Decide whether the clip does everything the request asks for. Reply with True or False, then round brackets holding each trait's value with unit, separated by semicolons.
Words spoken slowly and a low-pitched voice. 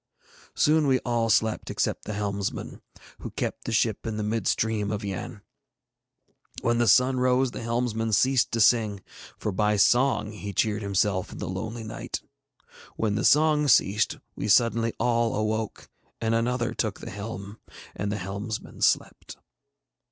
False (160 wpm; 110 Hz)